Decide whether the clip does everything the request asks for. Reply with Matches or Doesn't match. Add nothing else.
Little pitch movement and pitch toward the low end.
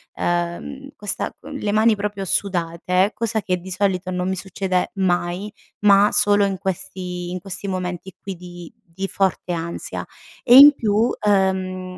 Doesn't match